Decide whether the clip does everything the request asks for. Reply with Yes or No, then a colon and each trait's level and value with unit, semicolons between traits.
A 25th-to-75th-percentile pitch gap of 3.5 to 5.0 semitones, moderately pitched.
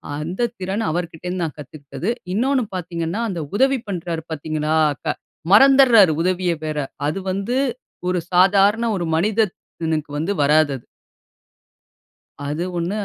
Yes: average, 4.3 semitones; medium, 180 Hz